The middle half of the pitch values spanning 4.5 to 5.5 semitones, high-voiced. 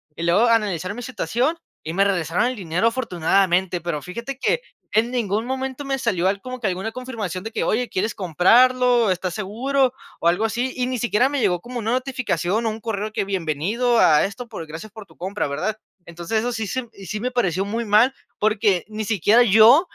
Yes: average, 4.8 semitones; high, 215 Hz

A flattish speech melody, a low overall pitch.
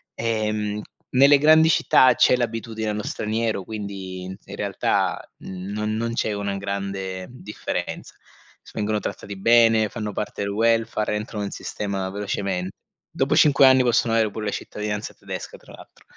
Yes: narrow, 2.3 semitones; low, 105 Hz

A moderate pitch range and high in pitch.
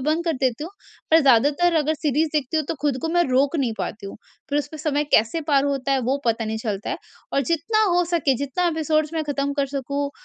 Yes: average, 3.1 semitones; very high, 285 Hz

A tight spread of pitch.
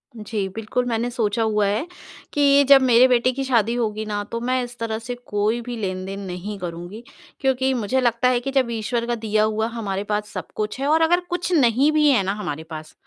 No: average, 3.4 semitones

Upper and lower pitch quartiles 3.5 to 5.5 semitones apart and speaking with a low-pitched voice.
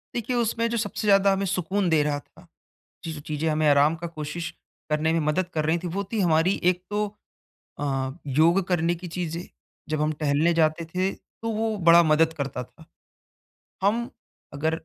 No: average, 3.8 semitones; medium, 165 Hz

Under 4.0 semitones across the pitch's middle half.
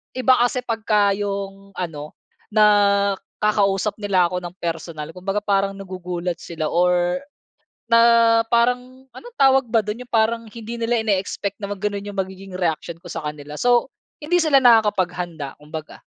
No: average, 4.3 semitones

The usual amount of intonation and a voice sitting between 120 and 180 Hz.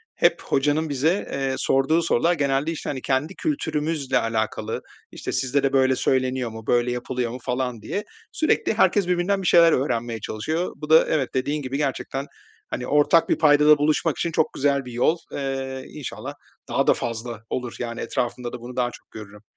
Yes: average, 3.8 semitones; low, 135 Hz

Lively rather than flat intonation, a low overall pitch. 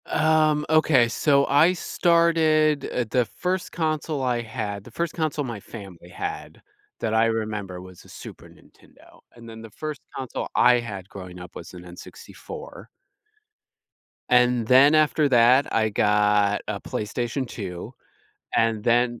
Yes: wide, 6.4 semitones; low, 120 Hz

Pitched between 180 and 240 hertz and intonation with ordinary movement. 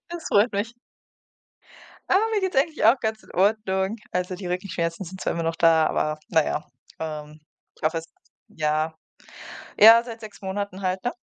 Yes: high, 190 Hz; average, 5.0 semitones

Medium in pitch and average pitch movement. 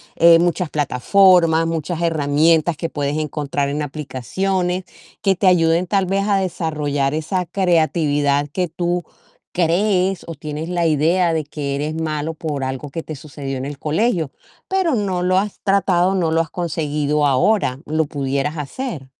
Yes: medium, 160 Hz; average, 3.6 semitones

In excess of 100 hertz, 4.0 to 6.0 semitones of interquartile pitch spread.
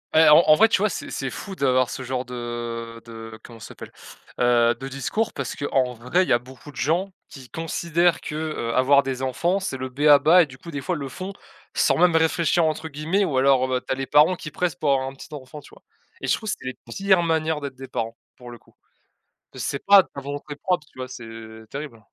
Yes: medium, 140 Hz; average, 4.3 semitones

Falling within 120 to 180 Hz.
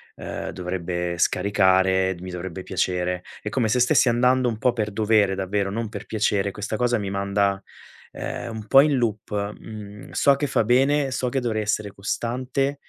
No: low, 105 Hz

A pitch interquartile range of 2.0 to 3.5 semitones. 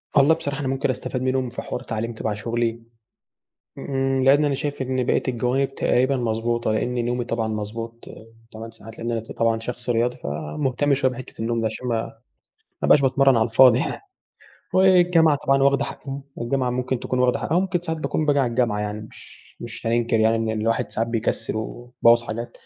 Yes: average, 2.9 semitones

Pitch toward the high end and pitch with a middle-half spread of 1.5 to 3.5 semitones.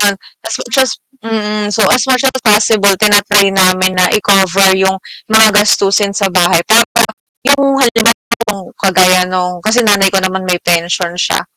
Yes: high, 200 Hz; average, 2.9 semitones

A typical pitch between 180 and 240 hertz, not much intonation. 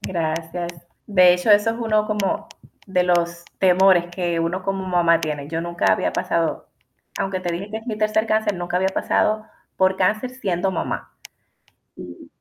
No: medium, 185 Hz; average, 3.3 semitones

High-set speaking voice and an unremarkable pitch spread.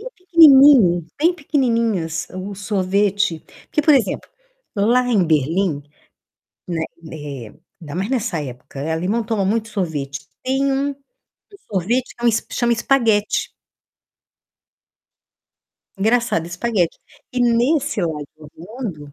No: high, 205 Hz; wide, 7.0 semitones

